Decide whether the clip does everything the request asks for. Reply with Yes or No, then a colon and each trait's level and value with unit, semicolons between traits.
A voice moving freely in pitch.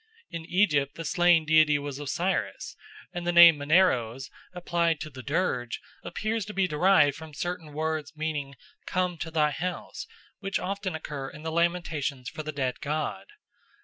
No: average, 3.3 semitones